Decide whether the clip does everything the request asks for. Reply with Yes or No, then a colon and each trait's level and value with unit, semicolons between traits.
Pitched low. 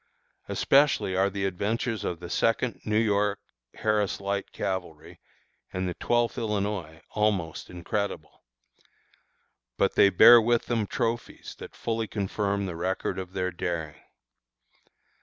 Yes: low, 100 Hz